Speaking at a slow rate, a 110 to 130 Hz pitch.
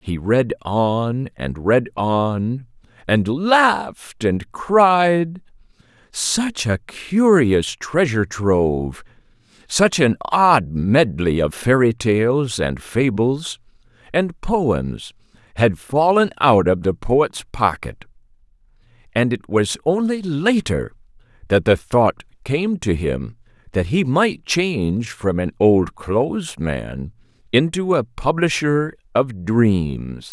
Yes: slow, 110 wpm; low, 125 Hz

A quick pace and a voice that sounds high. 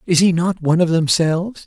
No: fast, 215 wpm; medium, 170 Hz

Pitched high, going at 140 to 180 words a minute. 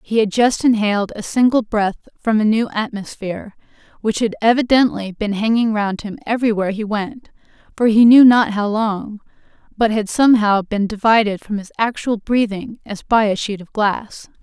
Yes: high, 215 Hz; average, 175 wpm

